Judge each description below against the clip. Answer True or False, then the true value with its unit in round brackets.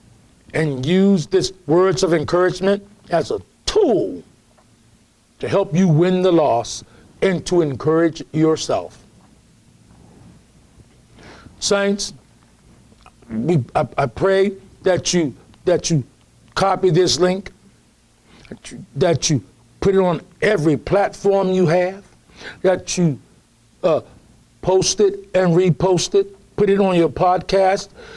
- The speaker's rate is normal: False (115 wpm)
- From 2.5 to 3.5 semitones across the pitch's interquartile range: False (4.2 semitones)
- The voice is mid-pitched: True (180 Hz)